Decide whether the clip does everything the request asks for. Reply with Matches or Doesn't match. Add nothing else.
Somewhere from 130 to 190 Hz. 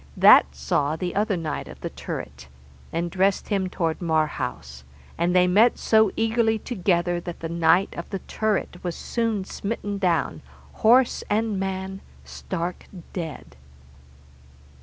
Matches